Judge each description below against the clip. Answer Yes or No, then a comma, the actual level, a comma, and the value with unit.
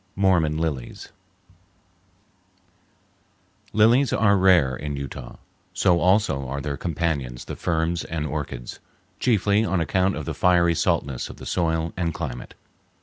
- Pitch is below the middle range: Yes, very low, 80 Hz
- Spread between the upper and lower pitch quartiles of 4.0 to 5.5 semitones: Yes, average, 4.7 semitones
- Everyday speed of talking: No, slow, 130 wpm